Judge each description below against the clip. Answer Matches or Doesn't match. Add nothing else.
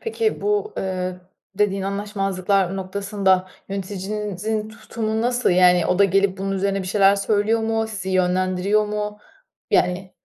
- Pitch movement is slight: Matches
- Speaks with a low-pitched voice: Doesn't match